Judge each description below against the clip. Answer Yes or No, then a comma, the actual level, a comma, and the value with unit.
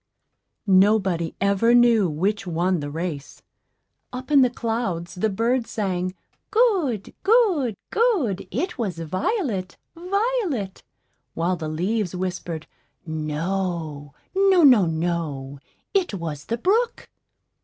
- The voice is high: Yes, high, 195 Hz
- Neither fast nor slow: No, slow, 110 wpm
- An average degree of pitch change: No, wide, 7.2 semitones